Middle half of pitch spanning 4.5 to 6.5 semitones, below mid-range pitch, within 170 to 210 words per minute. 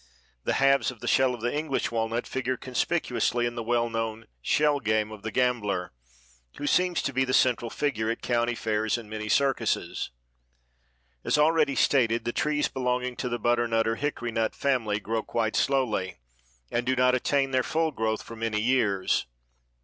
No: average, 3.0 semitones; low, 120 Hz; average, 175 wpm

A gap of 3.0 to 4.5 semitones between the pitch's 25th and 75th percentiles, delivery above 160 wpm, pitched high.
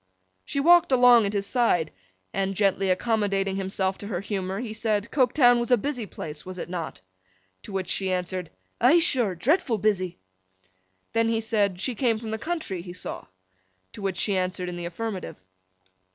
Yes: average, 4.0 semitones; average, 180 wpm; high, 205 Hz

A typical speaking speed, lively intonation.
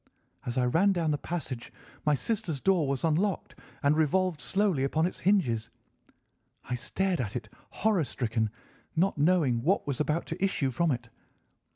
Yes: average, 165 wpm; wide, 6.2 semitones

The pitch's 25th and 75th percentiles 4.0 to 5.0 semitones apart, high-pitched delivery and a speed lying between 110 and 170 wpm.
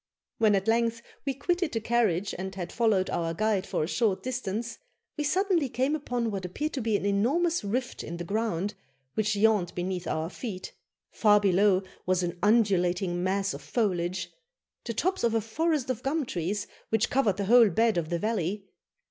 No: average, 4.3 semitones; high, 210 Hz; average, 185 wpm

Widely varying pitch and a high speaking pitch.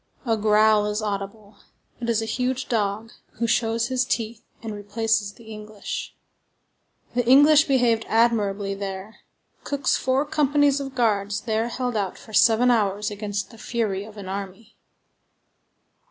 No: average, 2.8 semitones; high, 220 Hz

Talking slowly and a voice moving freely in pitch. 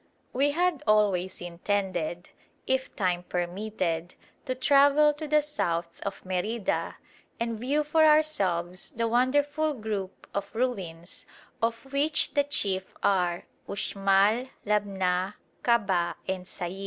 Yes: slow, 115 wpm; wide, 6.4 semitones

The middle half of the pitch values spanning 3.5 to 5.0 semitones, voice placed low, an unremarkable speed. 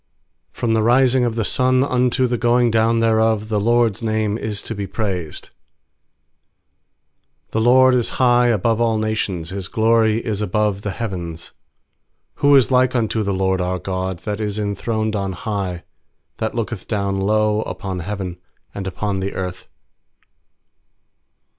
No: average, 3.0 semitones; low, 110 Hz; average, 150 wpm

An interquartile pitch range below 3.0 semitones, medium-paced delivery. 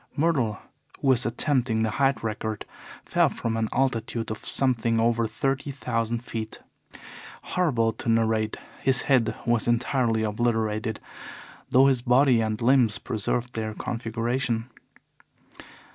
No: narrow, 2.5 semitones; slow, 125 wpm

